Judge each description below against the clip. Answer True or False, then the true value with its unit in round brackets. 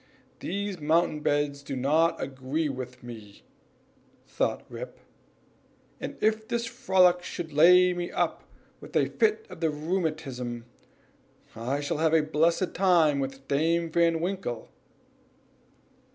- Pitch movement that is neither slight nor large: True (4.3 semitones)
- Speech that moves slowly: True (125 wpm)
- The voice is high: False (160 Hz)